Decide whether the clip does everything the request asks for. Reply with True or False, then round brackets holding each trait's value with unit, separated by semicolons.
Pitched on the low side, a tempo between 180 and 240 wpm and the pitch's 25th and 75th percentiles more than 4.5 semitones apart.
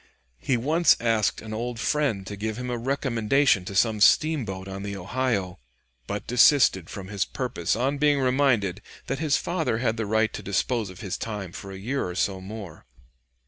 True (110 Hz; 185 wpm; 5.0 semitones)